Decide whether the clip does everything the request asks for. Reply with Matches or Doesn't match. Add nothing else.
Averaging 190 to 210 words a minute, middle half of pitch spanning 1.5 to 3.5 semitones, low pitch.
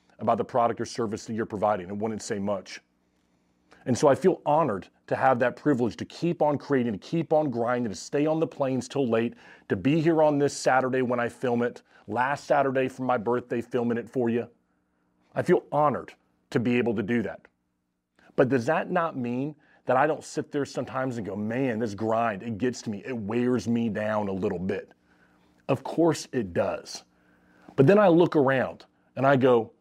Doesn't match